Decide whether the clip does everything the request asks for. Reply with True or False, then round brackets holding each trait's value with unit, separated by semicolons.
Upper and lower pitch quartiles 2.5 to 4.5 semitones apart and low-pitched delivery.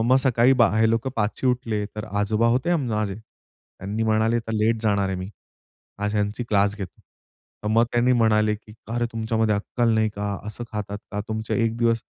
False (2.0 semitones; 110 Hz)